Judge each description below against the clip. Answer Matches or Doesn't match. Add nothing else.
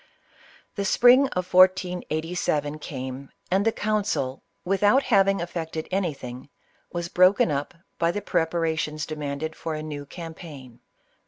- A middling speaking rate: Doesn't match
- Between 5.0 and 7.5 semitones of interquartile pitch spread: Doesn't match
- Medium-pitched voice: Matches